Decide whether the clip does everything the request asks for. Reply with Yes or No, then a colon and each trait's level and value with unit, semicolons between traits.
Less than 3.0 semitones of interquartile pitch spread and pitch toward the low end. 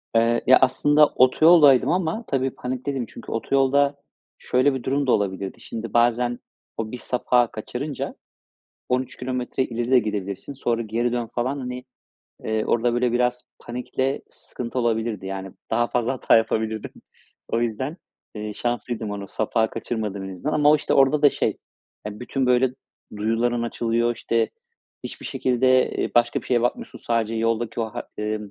Yes: narrow, 2.5 semitones; low, 120 Hz